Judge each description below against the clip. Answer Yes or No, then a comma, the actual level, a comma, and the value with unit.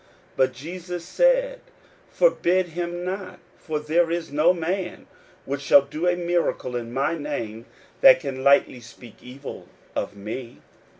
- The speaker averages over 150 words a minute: No, average, 145 wpm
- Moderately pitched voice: Yes, medium, 160 Hz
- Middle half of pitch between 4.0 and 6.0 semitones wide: Yes, average, 5.0 semitones